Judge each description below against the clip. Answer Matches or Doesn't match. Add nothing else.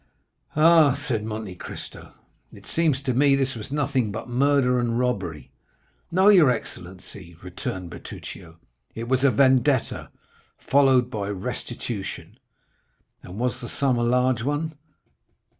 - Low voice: Matches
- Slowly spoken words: Matches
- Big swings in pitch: Doesn't match